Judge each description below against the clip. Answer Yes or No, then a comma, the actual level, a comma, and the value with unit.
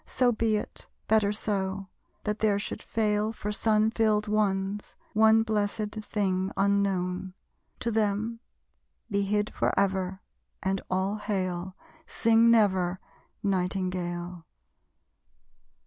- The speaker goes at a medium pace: No, slow, 105 wpm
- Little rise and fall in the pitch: Yes, narrow, 2.2 semitones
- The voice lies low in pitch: No, high, 205 Hz